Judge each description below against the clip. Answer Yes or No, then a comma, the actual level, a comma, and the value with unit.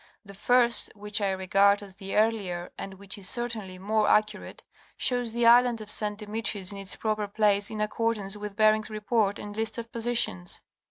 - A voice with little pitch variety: Yes, narrow, 2.1 semitones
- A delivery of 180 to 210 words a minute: Yes, average, 195 wpm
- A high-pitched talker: Yes, high, 210 Hz